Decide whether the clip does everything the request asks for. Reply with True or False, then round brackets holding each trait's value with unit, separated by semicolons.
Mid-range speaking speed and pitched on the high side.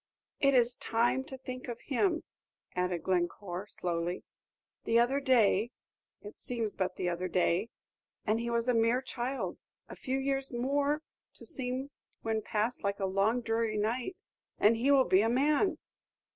True (160 wpm; 235 Hz)